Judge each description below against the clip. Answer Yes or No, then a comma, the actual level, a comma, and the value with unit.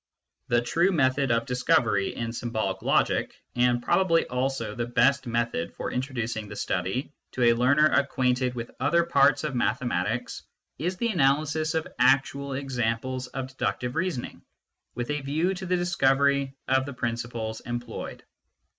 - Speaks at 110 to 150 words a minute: Yes, average, 145 wpm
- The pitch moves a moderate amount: Yes, average, 3.2 semitones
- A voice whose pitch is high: No, low, 130 Hz